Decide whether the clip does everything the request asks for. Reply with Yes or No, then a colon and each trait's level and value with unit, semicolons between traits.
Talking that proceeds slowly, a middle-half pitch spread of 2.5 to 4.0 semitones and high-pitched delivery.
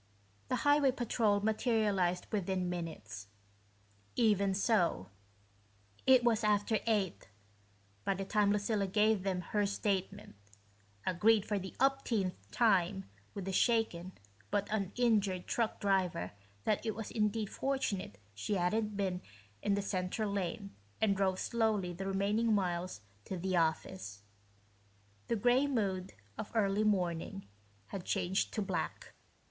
Yes: slow, 130 wpm; average, 2.8 semitones; high, 200 Hz